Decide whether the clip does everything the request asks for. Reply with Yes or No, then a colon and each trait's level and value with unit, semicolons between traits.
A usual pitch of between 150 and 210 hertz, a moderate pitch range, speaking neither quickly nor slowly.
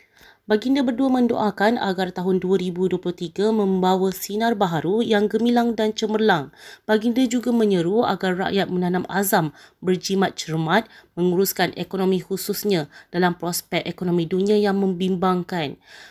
Yes: high, 190 Hz; average, 3.0 semitones; average, 115 wpm